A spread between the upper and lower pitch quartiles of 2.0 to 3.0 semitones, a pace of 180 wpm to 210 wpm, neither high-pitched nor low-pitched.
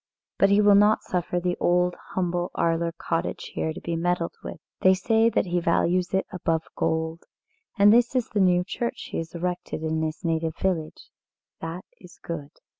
Yes: narrow, 2.4 semitones; average, 185 wpm; medium, 175 Hz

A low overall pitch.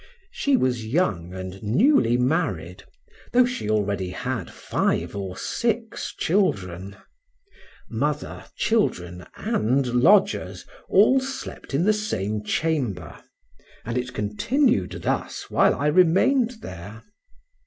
Yes: low, 125 Hz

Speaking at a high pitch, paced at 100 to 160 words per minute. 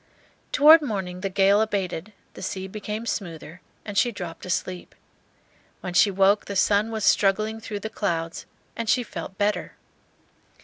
Yes: high, 200 Hz; average, 150 wpm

